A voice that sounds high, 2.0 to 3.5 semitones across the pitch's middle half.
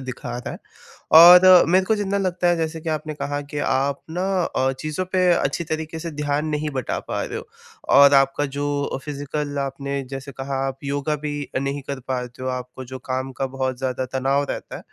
No: medium, 140 Hz; average, 2.9 semitones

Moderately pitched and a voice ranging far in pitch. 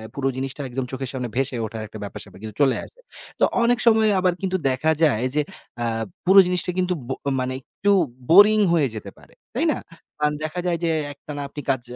Yes: medium, 145 Hz; wide, 5.9 semitones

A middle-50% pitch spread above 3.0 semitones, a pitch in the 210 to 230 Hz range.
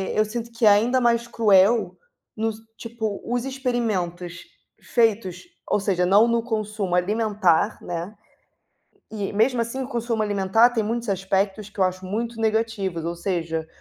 Yes: average, 3.4 semitones; high, 215 Hz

